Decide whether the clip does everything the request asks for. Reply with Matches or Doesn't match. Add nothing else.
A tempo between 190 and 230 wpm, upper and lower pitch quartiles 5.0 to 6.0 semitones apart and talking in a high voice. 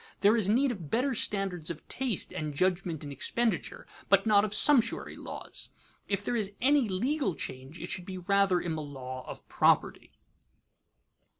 Doesn't match